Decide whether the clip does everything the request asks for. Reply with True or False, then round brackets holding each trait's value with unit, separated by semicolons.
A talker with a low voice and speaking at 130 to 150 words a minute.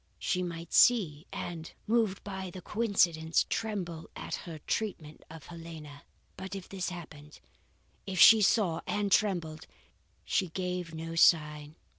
False (175 Hz; 135 wpm)